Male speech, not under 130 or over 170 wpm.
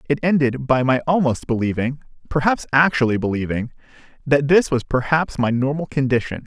Yes: male; average, 150 wpm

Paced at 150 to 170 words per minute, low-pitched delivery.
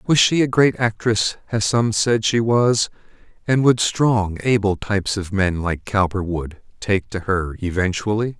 Yes: average, 155 wpm; low, 105 Hz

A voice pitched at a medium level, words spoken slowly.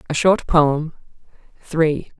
Yes: medium, 155 Hz; slow, 110 wpm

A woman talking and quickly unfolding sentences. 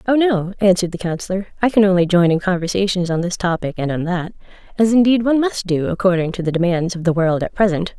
Yes: female; fast, 235 wpm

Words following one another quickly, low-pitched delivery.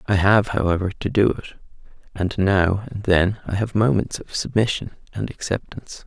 No: average, 170 wpm; low, 100 Hz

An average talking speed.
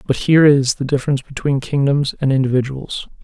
Yes: average, 165 wpm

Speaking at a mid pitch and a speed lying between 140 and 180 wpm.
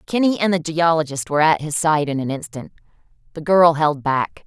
No: medium, 155 Hz; average, 200 wpm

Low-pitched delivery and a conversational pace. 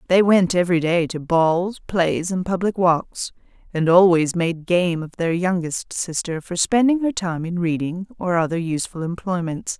No: medium, 175 Hz; average, 170 wpm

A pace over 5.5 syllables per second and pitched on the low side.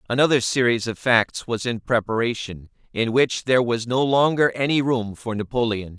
No: 5.0 syllables/s; low, 120 Hz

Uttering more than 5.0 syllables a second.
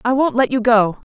Yes: 5.4 syllables/s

